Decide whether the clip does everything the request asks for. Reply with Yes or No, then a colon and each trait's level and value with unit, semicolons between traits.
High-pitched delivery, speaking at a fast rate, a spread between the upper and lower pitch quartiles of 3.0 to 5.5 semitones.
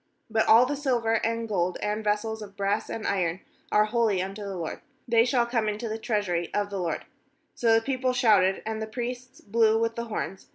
No: high, 220 Hz; fast, 210 wpm; narrow, 2.6 semitones